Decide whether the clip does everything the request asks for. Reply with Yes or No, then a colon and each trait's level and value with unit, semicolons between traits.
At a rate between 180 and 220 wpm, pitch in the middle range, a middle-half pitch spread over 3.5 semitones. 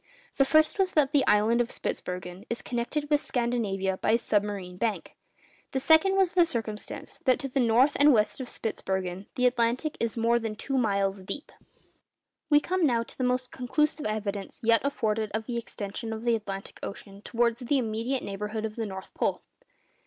No: average, 185 wpm; high, 230 Hz; average, 4.1 semitones